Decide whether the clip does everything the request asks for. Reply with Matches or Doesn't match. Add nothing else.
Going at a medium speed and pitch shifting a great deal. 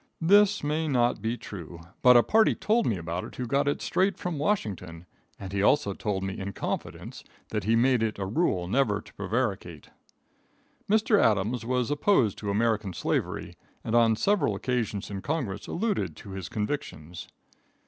Matches